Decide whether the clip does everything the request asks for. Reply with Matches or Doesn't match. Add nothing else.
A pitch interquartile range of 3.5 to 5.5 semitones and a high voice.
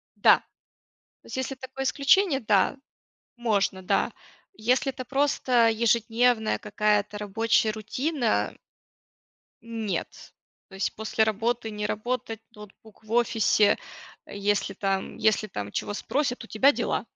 Doesn't match